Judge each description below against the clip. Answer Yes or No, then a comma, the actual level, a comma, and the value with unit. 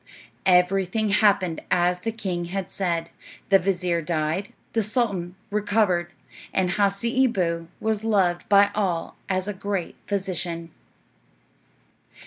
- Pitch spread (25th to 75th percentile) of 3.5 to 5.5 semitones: No, average, 2.8 semitones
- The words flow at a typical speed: No, slow, 115 wpm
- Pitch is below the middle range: No, high, 190 Hz